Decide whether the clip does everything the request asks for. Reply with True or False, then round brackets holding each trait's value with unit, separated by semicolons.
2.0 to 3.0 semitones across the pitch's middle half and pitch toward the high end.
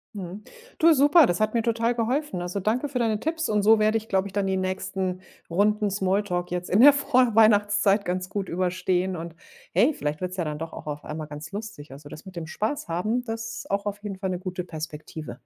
False (3.9 semitones; 195 Hz)